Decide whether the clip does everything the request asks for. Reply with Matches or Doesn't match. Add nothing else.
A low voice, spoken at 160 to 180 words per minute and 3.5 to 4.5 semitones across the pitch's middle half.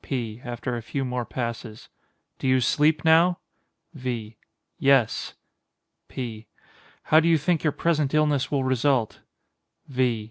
Doesn't match